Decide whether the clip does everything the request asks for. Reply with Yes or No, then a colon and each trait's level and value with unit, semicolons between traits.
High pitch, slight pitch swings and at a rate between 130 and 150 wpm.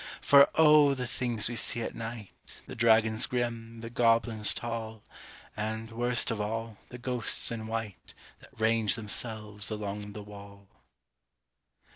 No: low, 115 Hz; narrow, 1.9 semitones; average, 140 wpm